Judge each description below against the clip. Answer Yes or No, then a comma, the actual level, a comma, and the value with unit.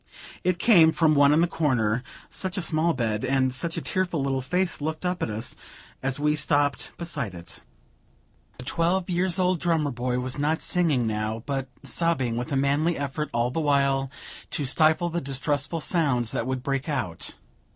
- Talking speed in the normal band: Yes, average, 185 wpm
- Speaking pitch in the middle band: Yes, medium, 145 Hz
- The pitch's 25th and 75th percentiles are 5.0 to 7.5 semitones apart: No, average, 4.5 semitones